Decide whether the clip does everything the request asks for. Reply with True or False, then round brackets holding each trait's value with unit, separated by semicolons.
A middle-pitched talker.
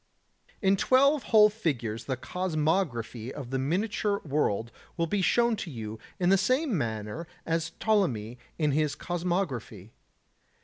True (160 Hz)